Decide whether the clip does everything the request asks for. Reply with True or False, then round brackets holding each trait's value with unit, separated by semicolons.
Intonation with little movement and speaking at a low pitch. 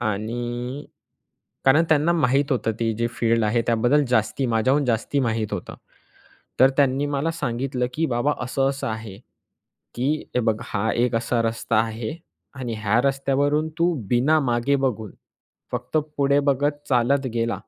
False (3.5 semitones; 125 Hz)